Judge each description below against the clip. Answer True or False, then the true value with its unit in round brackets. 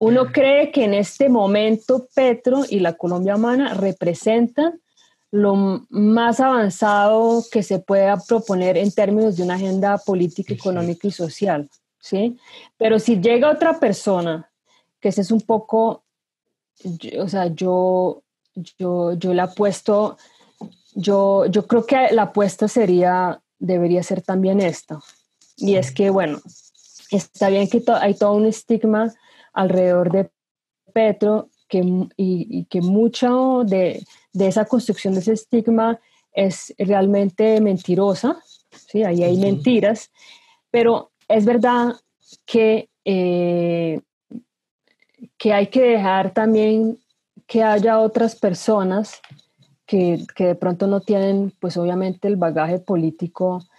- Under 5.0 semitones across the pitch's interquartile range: True (3.4 semitones)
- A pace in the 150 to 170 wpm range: False (130 wpm)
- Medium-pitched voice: False (205 Hz)